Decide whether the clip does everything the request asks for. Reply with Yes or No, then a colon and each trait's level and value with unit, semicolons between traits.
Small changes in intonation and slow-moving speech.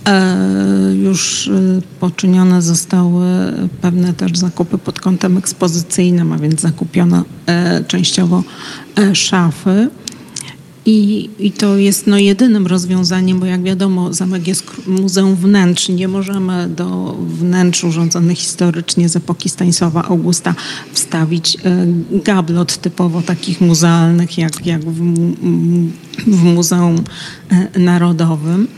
Yes: narrow, 1.7 semitones; slow, 100 wpm